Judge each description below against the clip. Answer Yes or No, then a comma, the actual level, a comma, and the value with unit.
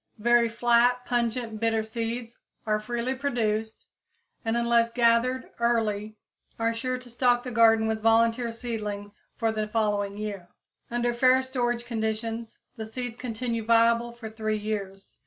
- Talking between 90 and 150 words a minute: Yes, average, 140 wpm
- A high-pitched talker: Yes, high, 230 Hz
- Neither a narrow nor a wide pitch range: No, narrow, 1.6 semitones